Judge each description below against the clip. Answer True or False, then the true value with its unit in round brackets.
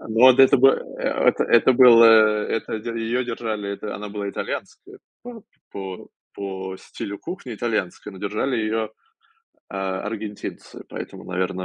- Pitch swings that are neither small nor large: True (3.2 semitones)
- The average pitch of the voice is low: True (110 Hz)